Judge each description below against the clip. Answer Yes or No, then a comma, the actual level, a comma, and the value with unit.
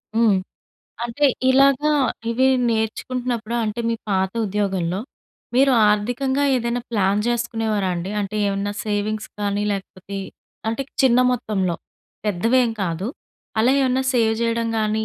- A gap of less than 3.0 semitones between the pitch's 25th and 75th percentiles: No, average, 3.3 semitones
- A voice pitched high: Yes, high, 220 Hz